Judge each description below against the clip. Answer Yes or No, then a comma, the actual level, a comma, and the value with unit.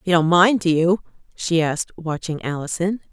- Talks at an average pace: Yes, average, 175 wpm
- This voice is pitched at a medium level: Yes, medium, 170 Hz